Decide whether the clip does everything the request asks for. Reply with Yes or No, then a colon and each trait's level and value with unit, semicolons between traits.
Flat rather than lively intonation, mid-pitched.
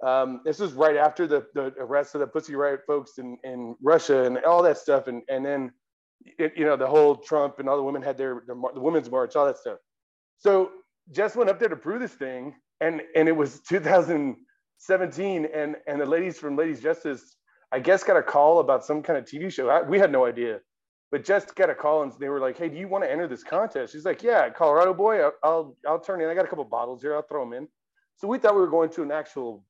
No: average, 4.1 semitones; medium, 150 Hz